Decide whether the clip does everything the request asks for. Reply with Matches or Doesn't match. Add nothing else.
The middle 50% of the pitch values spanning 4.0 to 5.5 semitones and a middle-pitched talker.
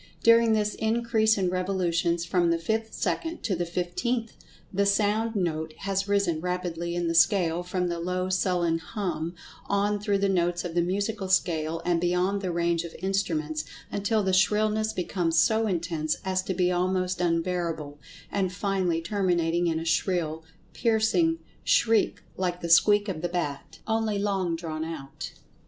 Doesn't match